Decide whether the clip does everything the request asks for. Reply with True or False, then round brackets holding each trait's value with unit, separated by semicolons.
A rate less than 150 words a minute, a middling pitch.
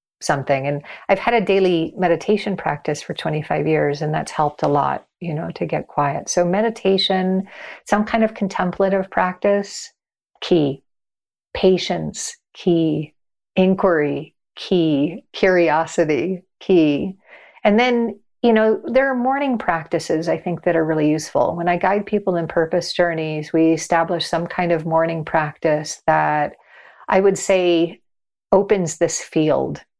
True (140 wpm; 175 Hz)